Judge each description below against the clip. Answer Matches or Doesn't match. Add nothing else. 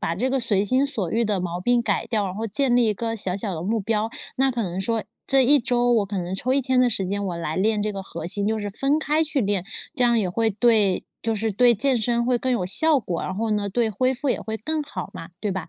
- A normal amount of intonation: Matches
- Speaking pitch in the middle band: Doesn't match